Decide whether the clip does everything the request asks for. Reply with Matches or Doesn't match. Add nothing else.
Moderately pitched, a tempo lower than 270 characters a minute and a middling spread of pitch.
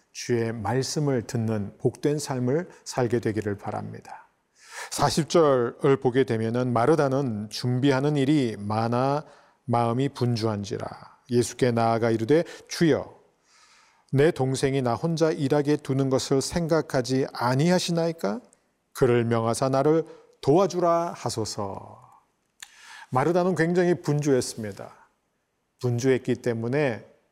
Doesn't match